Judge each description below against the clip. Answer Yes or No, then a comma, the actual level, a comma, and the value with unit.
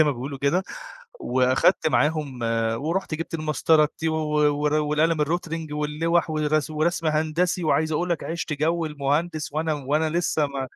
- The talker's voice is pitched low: No, medium, 155 Hz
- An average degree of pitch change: No, narrow, 1.7 semitones